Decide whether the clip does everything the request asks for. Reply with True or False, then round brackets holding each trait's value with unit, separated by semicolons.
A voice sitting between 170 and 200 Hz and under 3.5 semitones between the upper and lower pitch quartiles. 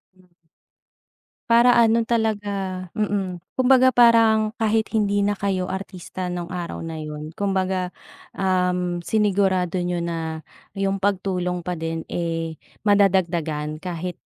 True (185 Hz; 2.8 semitones)